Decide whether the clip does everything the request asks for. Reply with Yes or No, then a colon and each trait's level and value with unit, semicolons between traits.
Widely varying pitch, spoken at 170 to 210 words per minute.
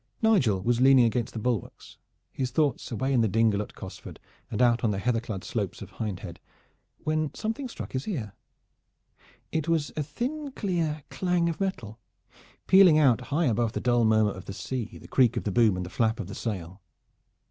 Yes: wide, 6.2 semitones; average, 195 wpm